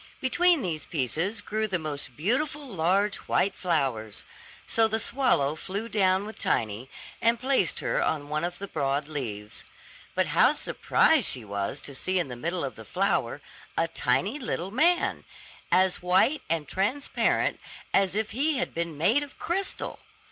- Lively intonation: Yes, wide, 7.4 semitones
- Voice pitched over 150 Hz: Yes, medium, 185 Hz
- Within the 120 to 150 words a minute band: No, average, 160 wpm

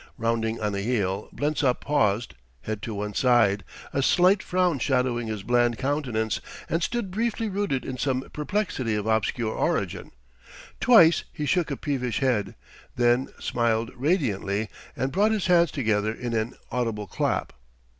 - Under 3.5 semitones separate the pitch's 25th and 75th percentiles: No, average, 5.3 semitones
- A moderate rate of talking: Yes, average, 150 wpm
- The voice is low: Yes, low, 125 Hz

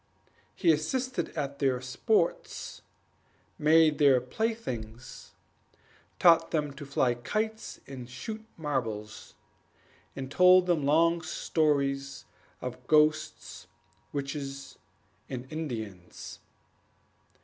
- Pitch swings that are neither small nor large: Yes, average, 4.2 semitones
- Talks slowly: Yes, slow, 90 wpm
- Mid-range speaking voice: Yes, medium, 145 Hz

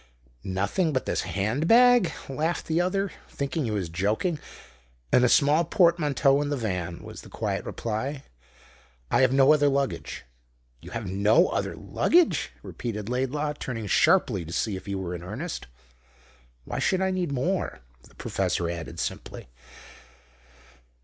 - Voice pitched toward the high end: No, low, 135 Hz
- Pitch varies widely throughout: Yes, wide, 7.8 semitones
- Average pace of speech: Yes, average, 150 wpm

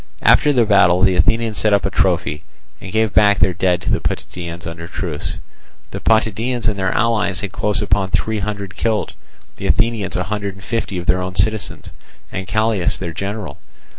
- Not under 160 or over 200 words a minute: Yes, average, 190 wpm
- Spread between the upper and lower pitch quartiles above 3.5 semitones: No, average, 3.0 semitones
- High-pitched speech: No, low, 100 Hz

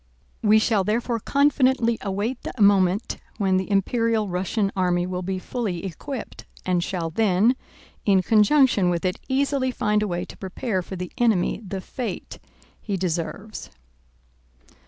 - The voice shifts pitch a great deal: No, average, 3.9 semitones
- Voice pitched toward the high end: Yes, high, 200 Hz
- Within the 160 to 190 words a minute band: No, average, 145 wpm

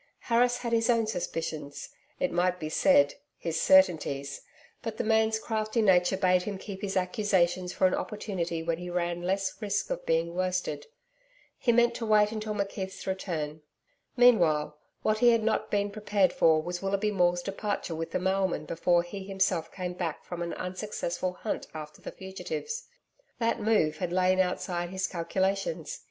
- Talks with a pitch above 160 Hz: Yes, high, 190 Hz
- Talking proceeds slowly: No, average, 170 wpm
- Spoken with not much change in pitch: No, average, 3.6 semitones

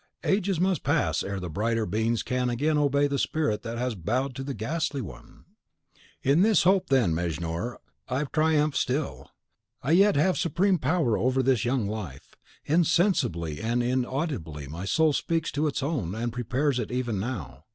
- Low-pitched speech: Yes, low, 130 Hz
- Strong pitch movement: Yes, wide, 6.0 semitones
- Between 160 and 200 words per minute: Yes, average, 170 wpm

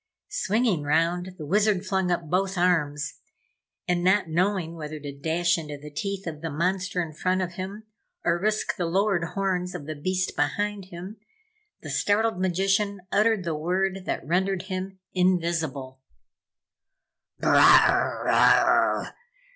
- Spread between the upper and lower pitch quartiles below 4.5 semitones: Yes, average, 3.0 semitones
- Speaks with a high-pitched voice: No, medium, 180 Hz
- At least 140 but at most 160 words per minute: Yes, average, 145 wpm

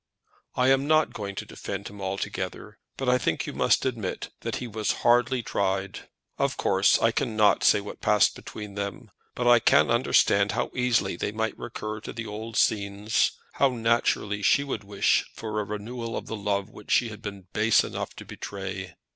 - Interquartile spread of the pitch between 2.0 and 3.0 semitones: Yes, average, 2.7 semitones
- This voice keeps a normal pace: Yes, average, 190 wpm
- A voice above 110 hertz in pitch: No, low, 105 Hz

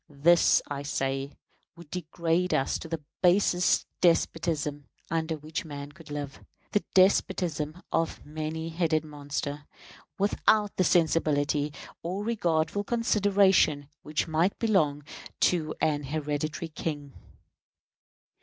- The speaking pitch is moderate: Yes, medium, 160 Hz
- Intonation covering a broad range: No, average, 3.3 semitones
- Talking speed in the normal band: No, slow, 115 wpm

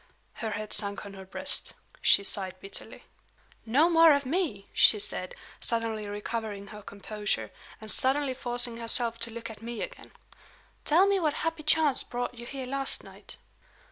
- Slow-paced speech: No, average, 165 wpm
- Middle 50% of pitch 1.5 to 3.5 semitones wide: No, average, 5.0 semitones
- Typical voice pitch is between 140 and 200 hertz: No, high, 230 Hz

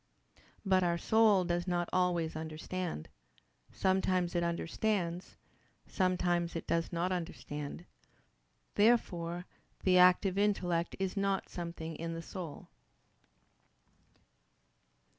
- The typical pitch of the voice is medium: Yes, medium, 175 Hz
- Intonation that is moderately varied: No, narrow, 1.8 semitones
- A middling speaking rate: No, slow, 100 wpm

